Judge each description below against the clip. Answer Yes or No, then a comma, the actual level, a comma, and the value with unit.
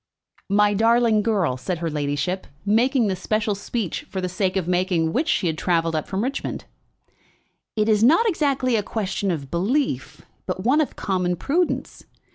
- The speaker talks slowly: No, average, 170 wpm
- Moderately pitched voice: No, high, 200 Hz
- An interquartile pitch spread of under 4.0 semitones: No, average, 4.8 semitones